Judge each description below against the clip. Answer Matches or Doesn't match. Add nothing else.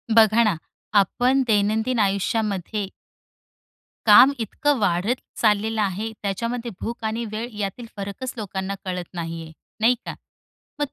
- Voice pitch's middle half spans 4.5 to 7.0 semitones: Doesn't match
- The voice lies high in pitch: Matches